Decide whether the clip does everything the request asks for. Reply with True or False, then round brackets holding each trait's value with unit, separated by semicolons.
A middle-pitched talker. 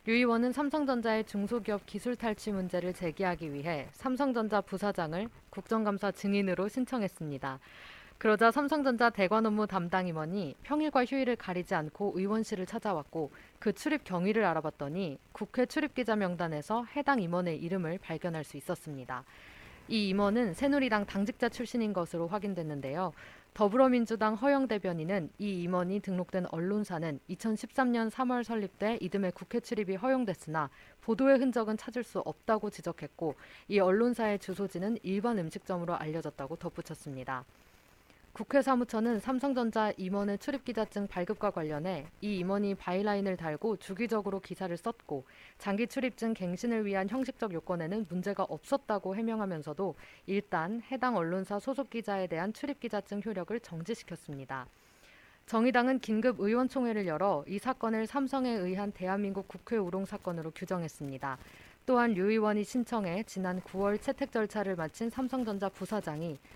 False (200 Hz)